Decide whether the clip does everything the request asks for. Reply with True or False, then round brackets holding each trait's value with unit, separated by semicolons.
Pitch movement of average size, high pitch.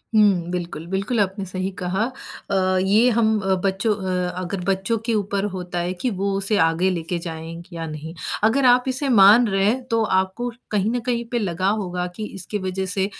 True (3.1 semitones; 195 Hz)